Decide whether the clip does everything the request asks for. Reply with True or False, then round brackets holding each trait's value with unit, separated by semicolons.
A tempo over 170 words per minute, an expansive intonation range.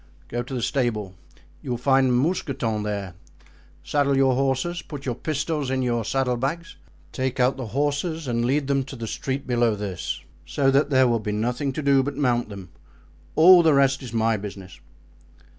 False (185 wpm; 3.1 semitones)